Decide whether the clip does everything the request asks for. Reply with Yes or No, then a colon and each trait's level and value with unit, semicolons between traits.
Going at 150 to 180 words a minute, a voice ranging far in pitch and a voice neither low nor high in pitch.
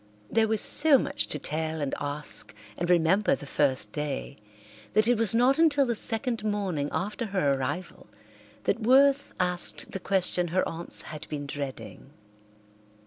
Yes: average, 155 wpm; wide, 7.1 semitones; medium, 180 Hz